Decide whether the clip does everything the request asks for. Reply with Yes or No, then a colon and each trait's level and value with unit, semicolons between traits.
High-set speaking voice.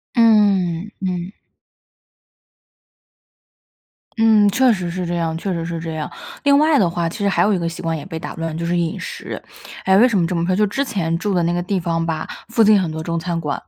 No: medium, 175 Hz